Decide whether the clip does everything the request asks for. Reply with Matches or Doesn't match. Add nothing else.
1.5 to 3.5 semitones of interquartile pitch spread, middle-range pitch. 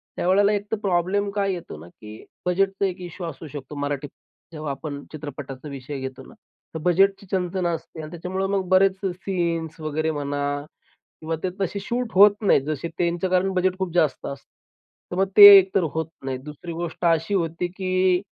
Doesn't match